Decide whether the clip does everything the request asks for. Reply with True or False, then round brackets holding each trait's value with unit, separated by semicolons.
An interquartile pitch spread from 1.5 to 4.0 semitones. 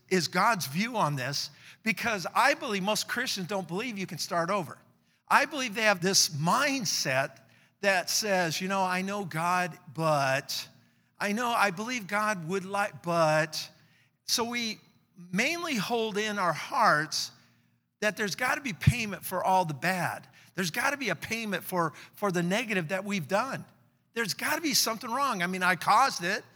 False (4.5 semitones)